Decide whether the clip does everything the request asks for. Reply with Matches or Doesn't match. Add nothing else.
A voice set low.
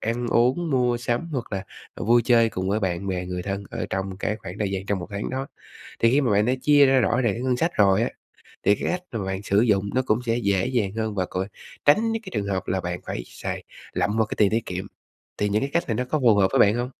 Matches